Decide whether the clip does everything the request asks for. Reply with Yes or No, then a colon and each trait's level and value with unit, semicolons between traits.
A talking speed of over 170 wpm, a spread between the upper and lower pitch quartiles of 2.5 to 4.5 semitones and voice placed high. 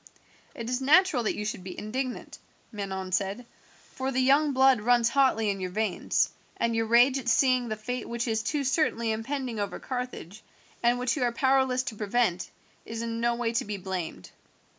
Yes: average, 190 wpm; average, 3.2 semitones; high, 235 Hz